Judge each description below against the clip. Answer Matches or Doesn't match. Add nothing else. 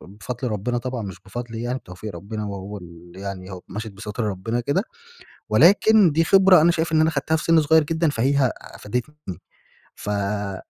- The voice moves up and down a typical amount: Doesn't match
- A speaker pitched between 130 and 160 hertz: Doesn't match